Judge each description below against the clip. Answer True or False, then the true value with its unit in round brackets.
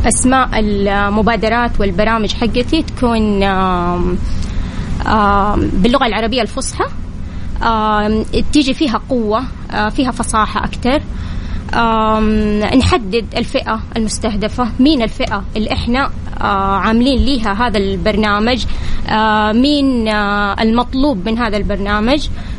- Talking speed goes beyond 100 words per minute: False (90 wpm)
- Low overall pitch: False (220 Hz)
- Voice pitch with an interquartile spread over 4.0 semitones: False (3.0 semitones)